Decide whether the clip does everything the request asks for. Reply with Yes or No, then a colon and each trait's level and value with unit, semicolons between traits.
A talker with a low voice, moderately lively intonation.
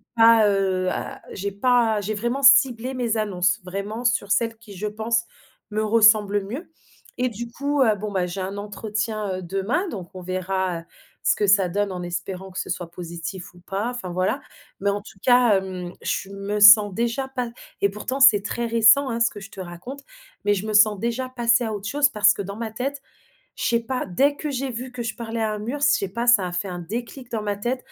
No: high, 215 Hz; average, 3.6 semitones